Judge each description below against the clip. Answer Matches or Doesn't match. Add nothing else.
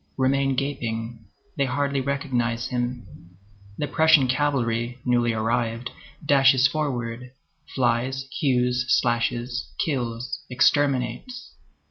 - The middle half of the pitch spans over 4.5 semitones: Doesn't match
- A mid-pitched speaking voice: Doesn't match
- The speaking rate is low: Matches